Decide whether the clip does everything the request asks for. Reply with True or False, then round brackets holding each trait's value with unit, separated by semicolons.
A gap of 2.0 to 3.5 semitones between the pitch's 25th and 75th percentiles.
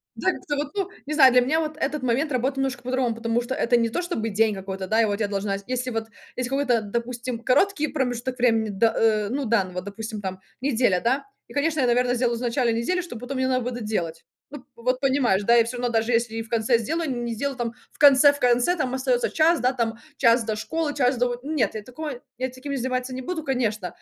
True (3.1 semitones)